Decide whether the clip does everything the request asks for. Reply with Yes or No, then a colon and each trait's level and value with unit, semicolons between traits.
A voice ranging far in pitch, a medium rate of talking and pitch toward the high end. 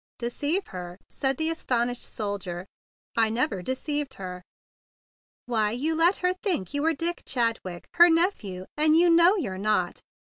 Yes: wide, 8.3 semitones; average, 155 wpm; very high, 255 Hz